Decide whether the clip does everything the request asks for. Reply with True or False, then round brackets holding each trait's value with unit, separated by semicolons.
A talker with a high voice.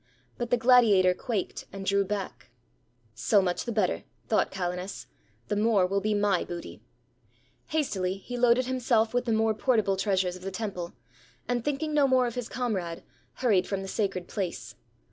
True (205 Hz)